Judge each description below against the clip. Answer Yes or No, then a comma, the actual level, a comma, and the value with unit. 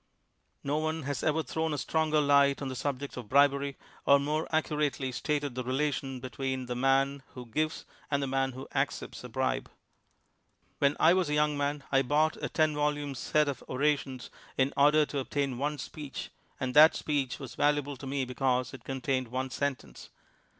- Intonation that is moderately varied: No, narrow, 2.1 semitones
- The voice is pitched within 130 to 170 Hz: Yes, medium, 140 Hz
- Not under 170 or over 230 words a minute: Yes, average, 190 wpm